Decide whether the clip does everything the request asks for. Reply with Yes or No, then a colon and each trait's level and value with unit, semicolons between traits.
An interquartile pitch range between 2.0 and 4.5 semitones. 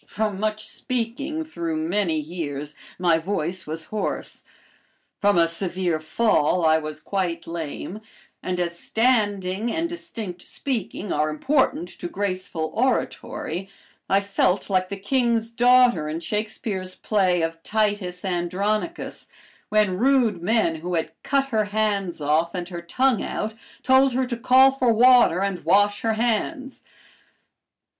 No: average, 5.1 semitones